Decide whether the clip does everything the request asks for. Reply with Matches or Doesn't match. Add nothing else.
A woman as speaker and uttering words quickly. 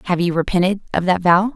Matches